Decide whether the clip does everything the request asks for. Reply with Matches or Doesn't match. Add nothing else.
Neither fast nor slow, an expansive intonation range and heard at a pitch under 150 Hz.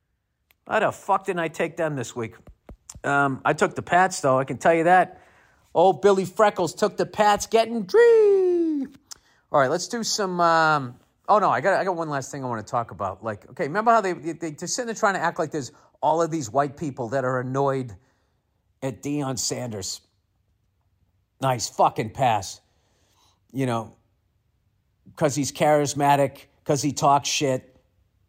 Matches